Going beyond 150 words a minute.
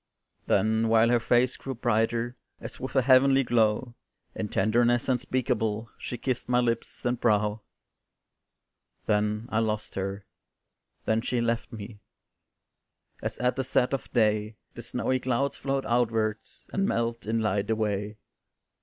No: average, 140 wpm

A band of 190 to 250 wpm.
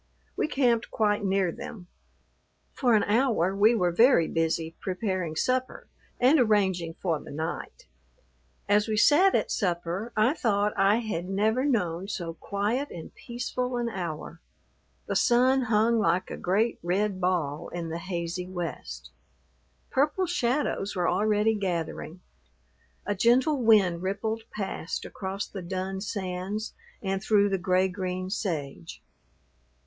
No: slow, 135 wpm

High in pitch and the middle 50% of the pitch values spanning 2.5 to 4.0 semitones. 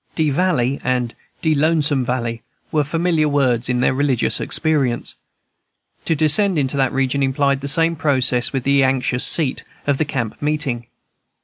No: medium, 140 Hz; average, 3.1 semitones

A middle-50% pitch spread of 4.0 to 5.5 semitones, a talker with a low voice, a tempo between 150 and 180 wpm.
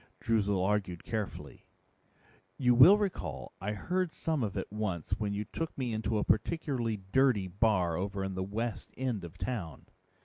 Yes: average, 4.4 semitones; low, 105 Hz; average, 165 wpm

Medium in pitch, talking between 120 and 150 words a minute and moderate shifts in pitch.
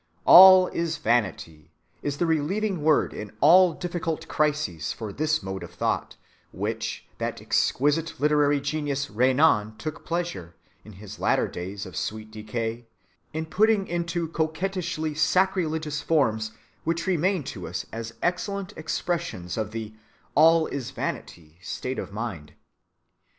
No: medium, 150 Hz; slow, 135 wpm; wide, 7.4 semitones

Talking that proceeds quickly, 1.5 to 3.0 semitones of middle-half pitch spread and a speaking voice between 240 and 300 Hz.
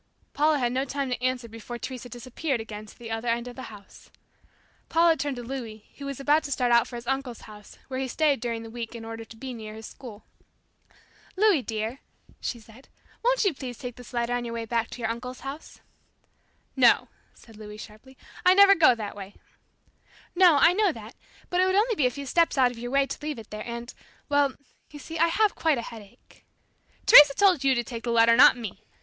No: fast, 225 wpm; average, 3.8 semitones; high, 245 Hz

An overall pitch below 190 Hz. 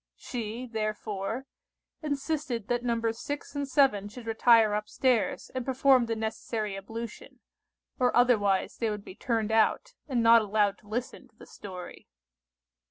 No: high, 230 Hz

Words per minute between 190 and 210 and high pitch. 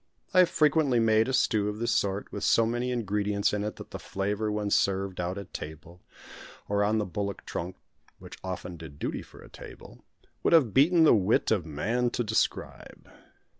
No: average, 195 wpm; low, 105 Hz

